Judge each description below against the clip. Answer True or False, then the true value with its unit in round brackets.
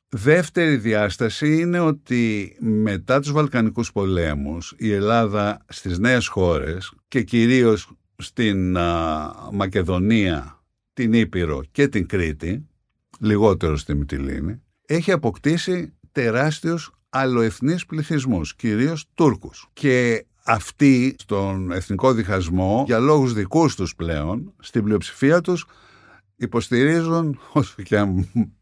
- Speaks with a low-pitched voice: True (115 Hz)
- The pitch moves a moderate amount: False (6.5 semitones)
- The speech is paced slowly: True (100 wpm)